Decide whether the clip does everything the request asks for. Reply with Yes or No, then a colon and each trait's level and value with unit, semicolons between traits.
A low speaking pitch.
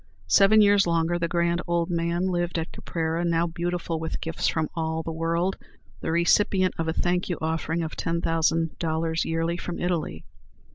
No: medium, 170 Hz